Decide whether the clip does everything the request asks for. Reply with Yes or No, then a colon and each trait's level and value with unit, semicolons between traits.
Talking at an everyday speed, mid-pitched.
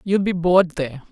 No: fast, 215 wpm; medium, 170 Hz